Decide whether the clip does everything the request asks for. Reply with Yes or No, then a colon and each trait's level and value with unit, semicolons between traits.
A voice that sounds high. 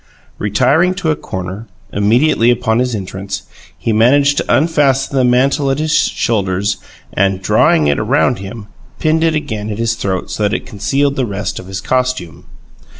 No: low, 115 Hz